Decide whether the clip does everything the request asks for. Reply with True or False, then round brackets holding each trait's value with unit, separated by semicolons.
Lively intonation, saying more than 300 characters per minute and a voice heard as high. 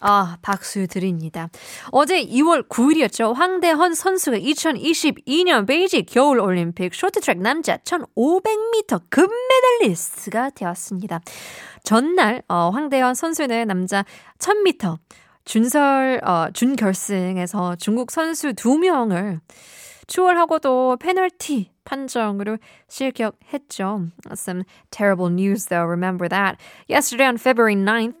True (8.7 semitones; 310 characters per minute; 240 Hz)